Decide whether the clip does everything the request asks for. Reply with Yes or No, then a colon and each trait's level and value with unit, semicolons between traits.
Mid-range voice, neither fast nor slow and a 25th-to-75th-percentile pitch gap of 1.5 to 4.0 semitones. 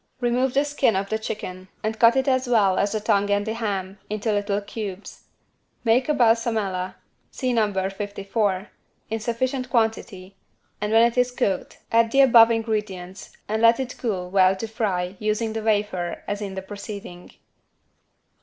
No: high, 215 Hz; average, 170 wpm; average, 2.8 semitones